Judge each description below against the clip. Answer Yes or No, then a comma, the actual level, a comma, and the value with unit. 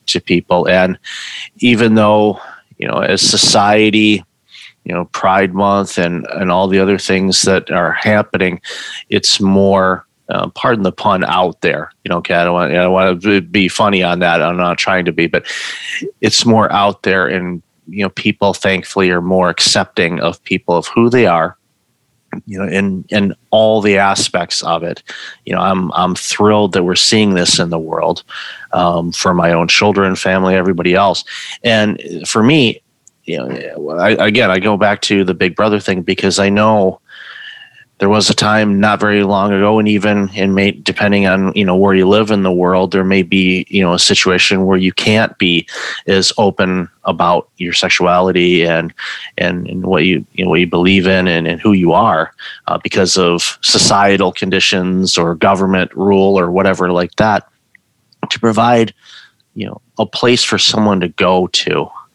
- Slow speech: No, average, 185 wpm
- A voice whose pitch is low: Yes, very low, 95 Hz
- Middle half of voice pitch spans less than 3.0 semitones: Yes, narrow, 2.4 semitones